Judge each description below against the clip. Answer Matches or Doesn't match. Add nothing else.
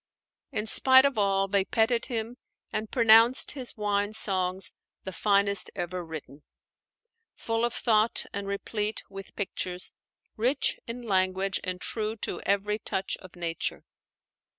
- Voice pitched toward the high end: Matches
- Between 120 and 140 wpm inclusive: Matches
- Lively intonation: Doesn't match